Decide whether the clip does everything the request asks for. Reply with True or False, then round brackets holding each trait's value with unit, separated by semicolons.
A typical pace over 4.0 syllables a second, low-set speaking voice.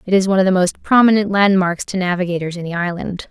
False (6.5 syllables/s; 185 Hz)